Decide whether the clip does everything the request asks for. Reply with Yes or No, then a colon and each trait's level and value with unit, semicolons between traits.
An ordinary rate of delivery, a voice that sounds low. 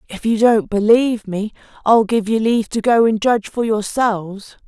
No: average, 190 wpm; high, 220 Hz